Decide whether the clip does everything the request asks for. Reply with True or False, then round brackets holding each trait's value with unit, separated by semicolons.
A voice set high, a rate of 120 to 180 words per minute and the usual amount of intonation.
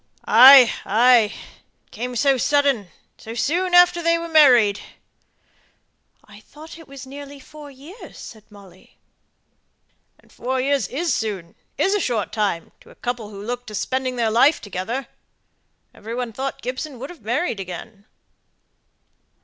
True (250 Hz; 150 wpm; 4.7 semitones)